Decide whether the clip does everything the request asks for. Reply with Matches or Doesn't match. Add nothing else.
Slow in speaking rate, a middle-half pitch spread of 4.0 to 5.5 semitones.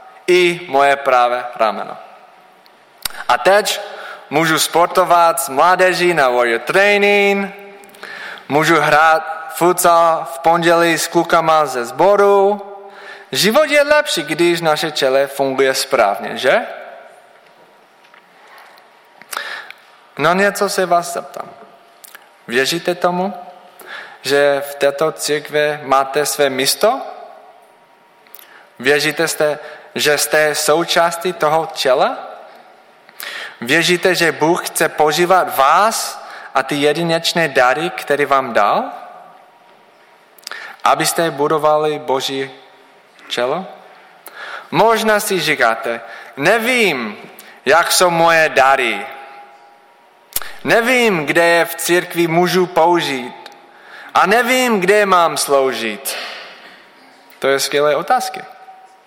Matches